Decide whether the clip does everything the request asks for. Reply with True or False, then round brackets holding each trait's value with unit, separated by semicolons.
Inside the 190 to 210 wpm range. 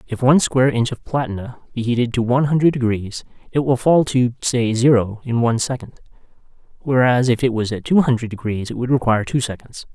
True (205 wpm)